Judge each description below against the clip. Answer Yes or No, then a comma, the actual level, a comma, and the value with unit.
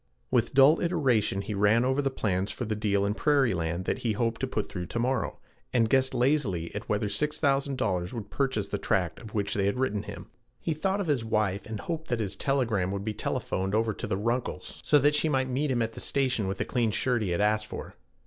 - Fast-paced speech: Yes, fast, 235 wpm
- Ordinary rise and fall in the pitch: Yes, average, 4.7 semitones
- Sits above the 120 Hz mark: No, low, 115 Hz